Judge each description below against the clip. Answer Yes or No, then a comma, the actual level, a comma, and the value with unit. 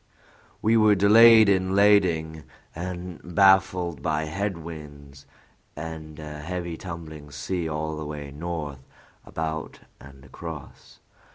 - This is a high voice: No, very low, 80 Hz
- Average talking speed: No, slow, 115 wpm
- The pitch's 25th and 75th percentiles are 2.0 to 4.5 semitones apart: Yes, average, 3.4 semitones